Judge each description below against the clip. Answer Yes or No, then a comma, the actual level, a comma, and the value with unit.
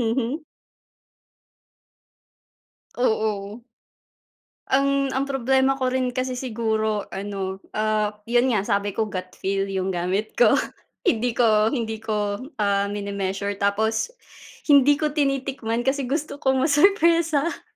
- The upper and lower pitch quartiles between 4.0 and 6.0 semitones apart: Yes, average, 4.7 semitones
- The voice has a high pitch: Yes, high, 225 Hz